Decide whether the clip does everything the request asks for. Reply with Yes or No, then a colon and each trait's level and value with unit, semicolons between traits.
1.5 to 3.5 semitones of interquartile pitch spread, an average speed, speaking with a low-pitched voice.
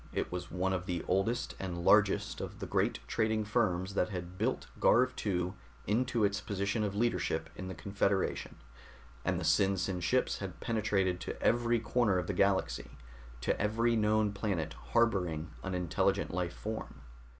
Yes: average, 3.2 semitones; average, 160 wpm; low, 100 Hz